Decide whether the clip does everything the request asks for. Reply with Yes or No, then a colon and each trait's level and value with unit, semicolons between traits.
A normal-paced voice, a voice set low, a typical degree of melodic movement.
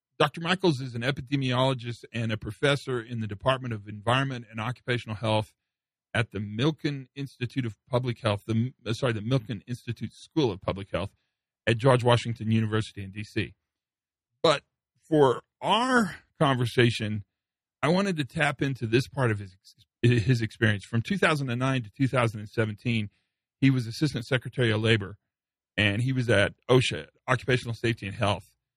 Yes: average, 150 wpm; low, 120 Hz; average, 3.4 semitones